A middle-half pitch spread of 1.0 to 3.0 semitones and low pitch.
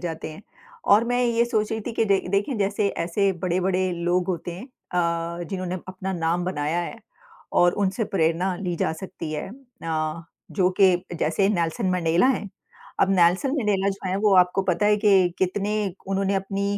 No: narrow, 2.6 semitones; medium, 185 Hz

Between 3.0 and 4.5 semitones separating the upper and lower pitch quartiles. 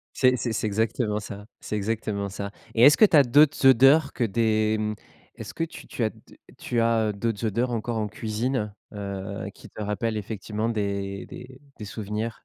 No: narrow, 2.5 semitones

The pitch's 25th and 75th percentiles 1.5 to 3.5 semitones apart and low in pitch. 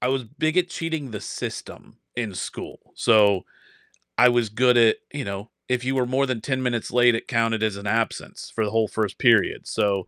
Yes: average, 3.1 semitones; low, 120 Hz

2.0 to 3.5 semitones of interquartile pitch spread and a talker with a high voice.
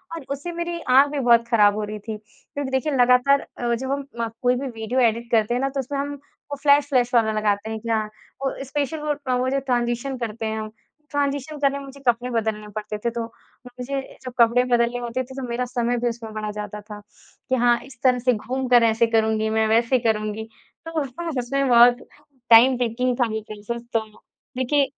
Yes: average, 3.2 semitones; high, 245 Hz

